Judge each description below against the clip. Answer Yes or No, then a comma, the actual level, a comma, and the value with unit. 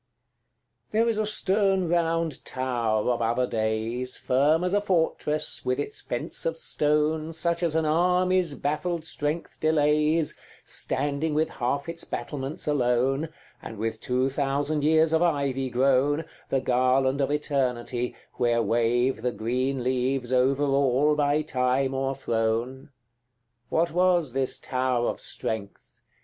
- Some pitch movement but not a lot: Yes, average, 4.0 semitones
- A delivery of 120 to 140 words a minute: Yes, slow, 135 wpm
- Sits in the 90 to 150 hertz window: Yes, medium, 140 Hz